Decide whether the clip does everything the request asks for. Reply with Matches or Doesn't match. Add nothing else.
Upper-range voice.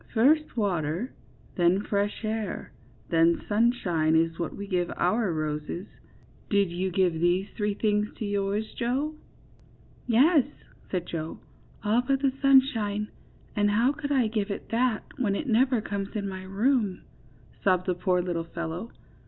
Matches